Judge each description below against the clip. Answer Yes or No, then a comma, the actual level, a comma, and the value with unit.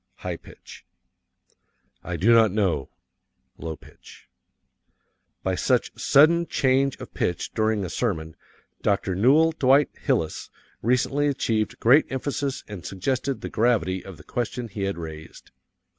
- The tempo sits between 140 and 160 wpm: Yes, average, 145 wpm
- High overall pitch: No, low, 110 Hz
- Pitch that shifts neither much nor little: No, wide, 6.3 semitones